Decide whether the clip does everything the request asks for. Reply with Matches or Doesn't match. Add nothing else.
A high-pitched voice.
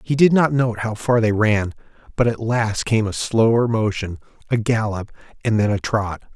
Doesn't match